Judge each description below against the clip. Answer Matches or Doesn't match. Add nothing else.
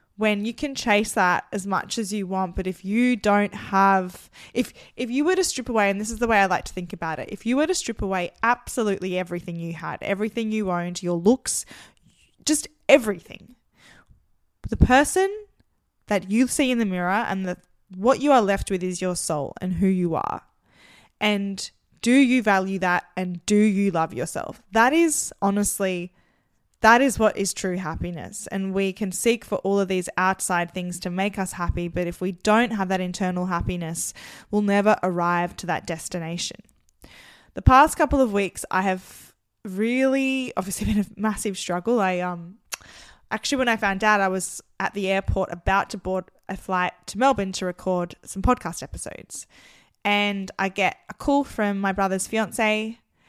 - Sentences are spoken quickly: Doesn't match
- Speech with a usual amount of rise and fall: Matches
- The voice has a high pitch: Matches